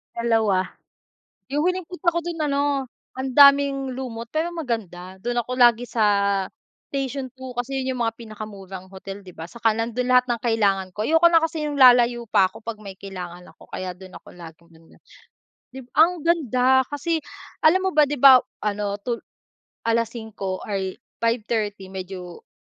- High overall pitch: Yes, high, 235 Hz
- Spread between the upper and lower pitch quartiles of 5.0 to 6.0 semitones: Yes, wide, 5.6 semitones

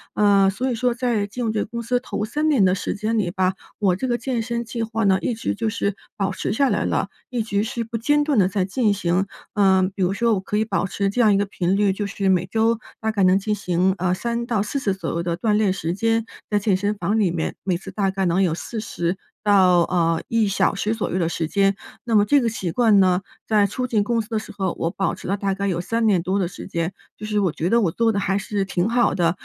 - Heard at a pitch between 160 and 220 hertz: Yes, high, 205 Hz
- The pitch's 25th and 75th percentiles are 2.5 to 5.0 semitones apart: Yes, average, 3.2 semitones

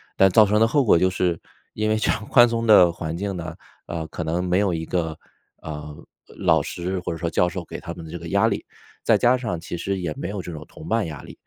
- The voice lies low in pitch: Yes, very low, 90 Hz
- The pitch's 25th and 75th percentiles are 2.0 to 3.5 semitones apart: No, average, 3.9 semitones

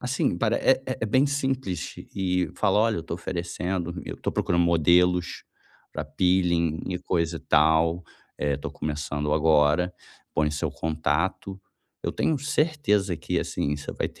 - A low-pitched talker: Yes, very low, 85 Hz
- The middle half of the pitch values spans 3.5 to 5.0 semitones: Yes, average, 4.3 semitones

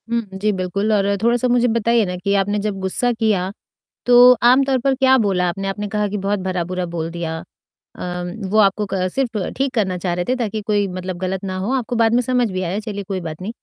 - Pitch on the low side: No, high, 205 Hz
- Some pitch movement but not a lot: Yes, average, 4.0 semitones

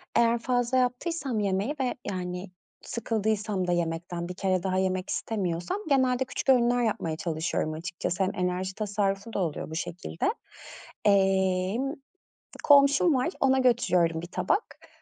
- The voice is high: Yes, high, 195 Hz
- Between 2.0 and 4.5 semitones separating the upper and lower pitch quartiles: No, average, 5.3 semitones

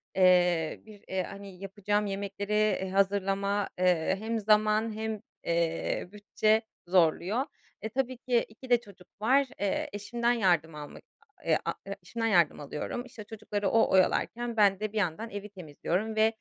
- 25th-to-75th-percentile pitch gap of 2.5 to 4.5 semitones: Yes, average, 2.9 semitones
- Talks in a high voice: Yes, high, 205 Hz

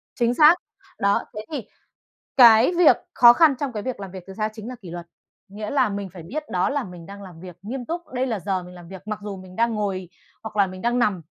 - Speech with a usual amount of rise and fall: Yes, average, 4.7 semitones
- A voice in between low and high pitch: No, high, 210 Hz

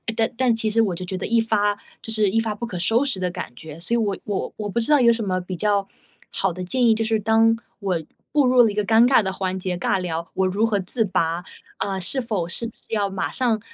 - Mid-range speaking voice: No, high, 210 Hz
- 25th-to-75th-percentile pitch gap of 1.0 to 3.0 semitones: No, average, 3.4 semitones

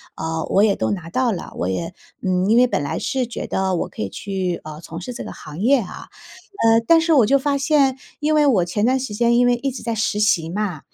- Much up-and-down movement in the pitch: Yes, wide, 6.4 semitones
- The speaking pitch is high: Yes, high, 215 Hz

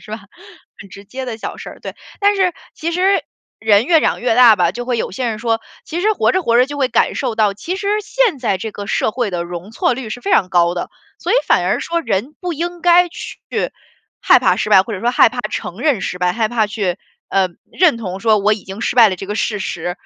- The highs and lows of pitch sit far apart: Yes, wide, 7.5 semitones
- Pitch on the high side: Yes, high, 230 Hz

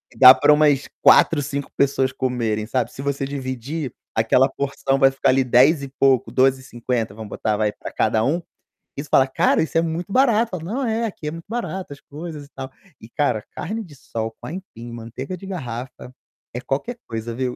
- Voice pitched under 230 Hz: Yes, low, 135 Hz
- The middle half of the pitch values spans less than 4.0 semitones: No, average, 4.3 semitones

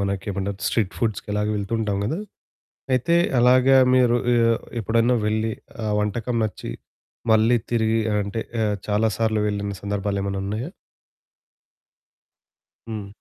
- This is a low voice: Yes, low, 110 Hz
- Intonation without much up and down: Yes, narrow, 2.3 semitones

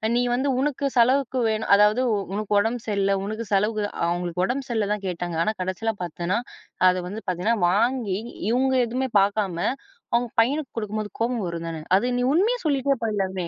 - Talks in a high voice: Yes, high, 215 Hz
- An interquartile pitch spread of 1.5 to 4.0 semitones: No, average, 4.4 semitones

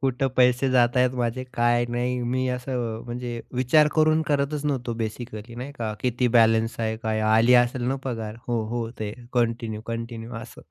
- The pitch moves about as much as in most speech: No, narrow, 1.9 semitones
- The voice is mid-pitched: No, low, 120 Hz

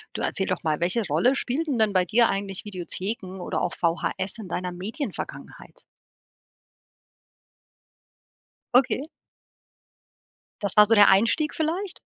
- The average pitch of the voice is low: No, high, 205 Hz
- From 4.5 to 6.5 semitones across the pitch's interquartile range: Yes, average, 4.8 semitones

